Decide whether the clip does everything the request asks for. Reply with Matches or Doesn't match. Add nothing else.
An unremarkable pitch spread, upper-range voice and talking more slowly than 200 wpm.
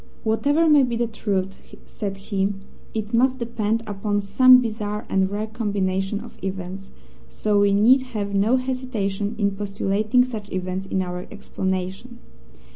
Matches